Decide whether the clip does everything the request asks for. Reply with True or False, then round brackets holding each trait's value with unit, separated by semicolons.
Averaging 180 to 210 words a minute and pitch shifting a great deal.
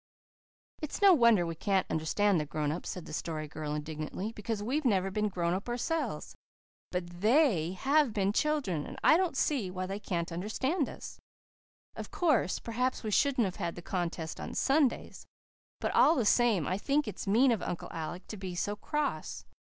True (185 wpm; 6.7 semitones)